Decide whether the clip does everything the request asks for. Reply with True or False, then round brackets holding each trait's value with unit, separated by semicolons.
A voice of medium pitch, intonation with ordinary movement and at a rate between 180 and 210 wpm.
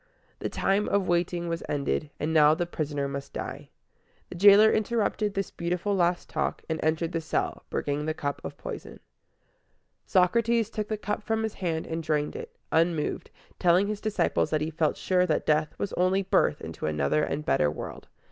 True (170 Hz; 4.6 semitones; 185 wpm)